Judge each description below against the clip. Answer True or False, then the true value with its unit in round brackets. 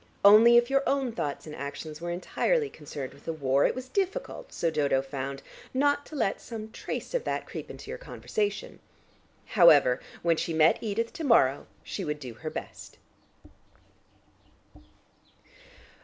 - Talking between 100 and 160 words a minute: True (155 wpm)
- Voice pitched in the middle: True (175 Hz)